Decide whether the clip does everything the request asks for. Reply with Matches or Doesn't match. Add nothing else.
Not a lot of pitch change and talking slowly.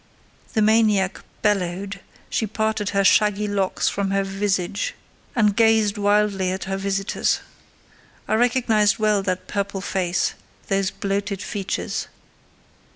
Matches